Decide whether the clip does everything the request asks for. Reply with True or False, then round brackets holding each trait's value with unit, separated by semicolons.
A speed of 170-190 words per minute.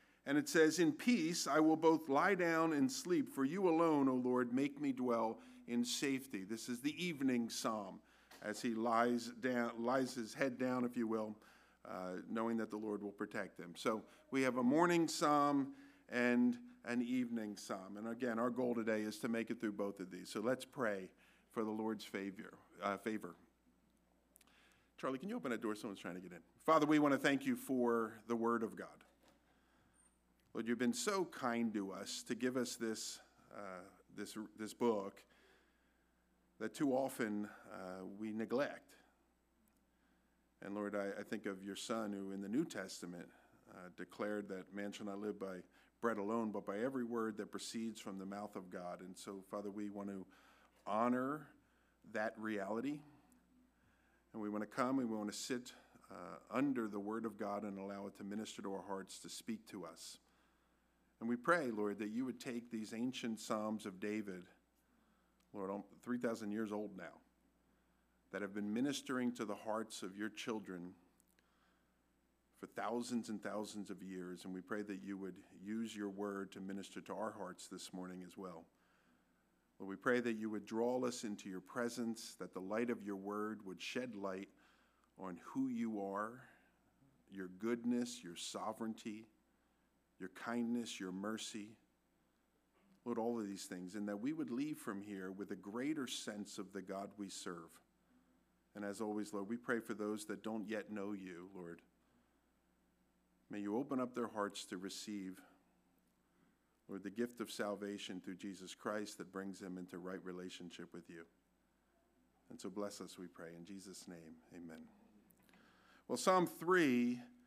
True (180 wpm)